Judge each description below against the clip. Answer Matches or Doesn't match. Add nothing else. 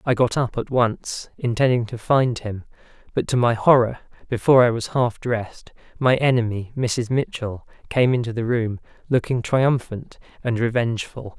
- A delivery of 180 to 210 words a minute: Doesn't match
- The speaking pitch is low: Matches